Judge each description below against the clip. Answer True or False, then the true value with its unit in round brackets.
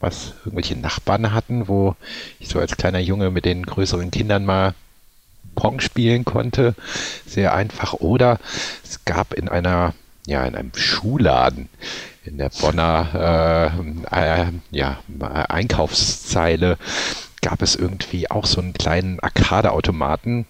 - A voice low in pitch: True (90 Hz)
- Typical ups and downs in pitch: True (3.8 semitones)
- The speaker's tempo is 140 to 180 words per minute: False (130 wpm)